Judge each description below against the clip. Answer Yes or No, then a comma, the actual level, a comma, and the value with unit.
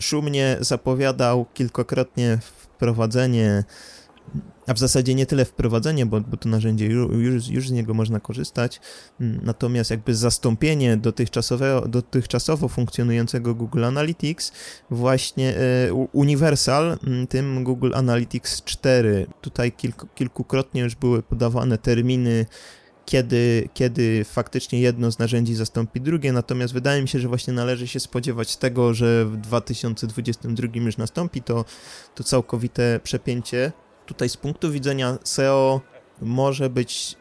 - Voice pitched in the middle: No, low, 125 Hz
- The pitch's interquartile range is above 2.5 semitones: No, narrow, 2.0 semitones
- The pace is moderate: Yes, average, 120 wpm